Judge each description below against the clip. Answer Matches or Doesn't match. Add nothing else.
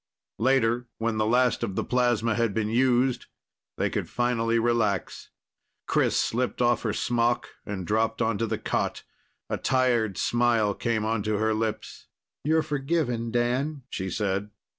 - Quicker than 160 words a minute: Doesn't match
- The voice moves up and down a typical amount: Doesn't match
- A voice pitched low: Matches